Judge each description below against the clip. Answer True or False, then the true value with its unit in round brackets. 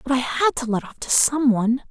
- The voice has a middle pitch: False (255 Hz)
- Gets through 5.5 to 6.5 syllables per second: True (5.6 syllables/s)